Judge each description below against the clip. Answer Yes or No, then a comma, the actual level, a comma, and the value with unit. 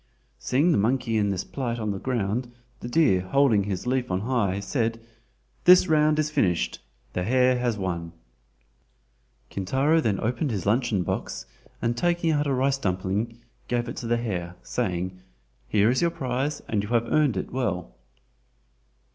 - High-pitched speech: No, low, 115 Hz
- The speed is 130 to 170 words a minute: Yes, average, 165 wpm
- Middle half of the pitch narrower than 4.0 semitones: No, average, 5.3 semitones